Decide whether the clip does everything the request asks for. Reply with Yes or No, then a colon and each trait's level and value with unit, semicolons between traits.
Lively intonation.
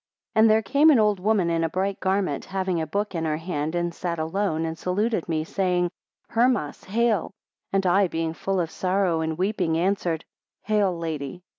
No: average, 3.6 semitones